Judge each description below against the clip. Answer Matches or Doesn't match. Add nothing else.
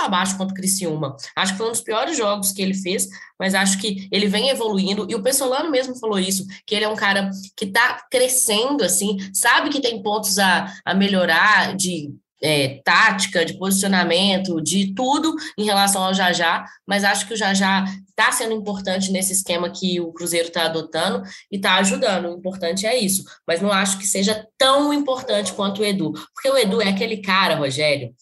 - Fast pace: Matches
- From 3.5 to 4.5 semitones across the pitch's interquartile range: Doesn't match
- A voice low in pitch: Doesn't match